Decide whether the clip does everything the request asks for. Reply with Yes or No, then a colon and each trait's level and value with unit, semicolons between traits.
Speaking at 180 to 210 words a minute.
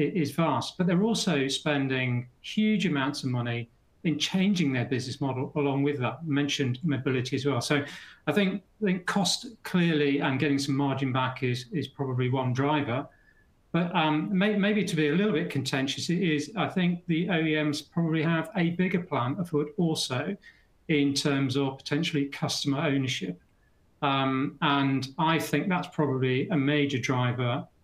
No: average, 170 wpm